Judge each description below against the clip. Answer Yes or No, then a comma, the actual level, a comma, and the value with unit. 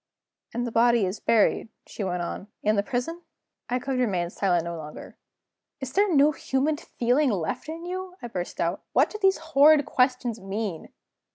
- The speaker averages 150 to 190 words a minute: Yes, average, 180 wpm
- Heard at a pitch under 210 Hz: No, high, 240 Hz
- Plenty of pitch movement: Yes, wide, 7.2 semitones